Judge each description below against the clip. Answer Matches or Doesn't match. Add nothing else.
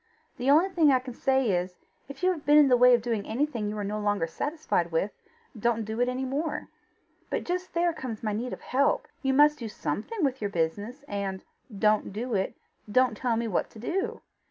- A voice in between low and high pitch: Doesn't match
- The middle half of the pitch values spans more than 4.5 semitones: Matches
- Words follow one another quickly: Matches